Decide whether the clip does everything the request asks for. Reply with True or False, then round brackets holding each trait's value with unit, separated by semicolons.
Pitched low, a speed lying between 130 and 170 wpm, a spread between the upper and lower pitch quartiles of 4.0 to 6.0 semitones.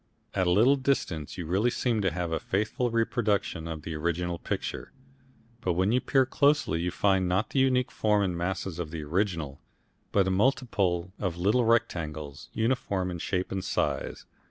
False (95 Hz; 180 wpm; 4.8 semitones)